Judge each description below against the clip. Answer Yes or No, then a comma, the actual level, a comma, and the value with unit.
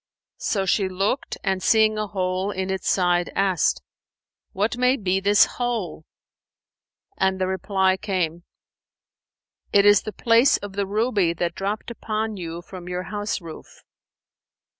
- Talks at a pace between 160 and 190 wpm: No, average, 140 wpm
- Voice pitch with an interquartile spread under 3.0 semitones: Yes, narrow, 2.6 semitones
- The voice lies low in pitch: No, high, 195 Hz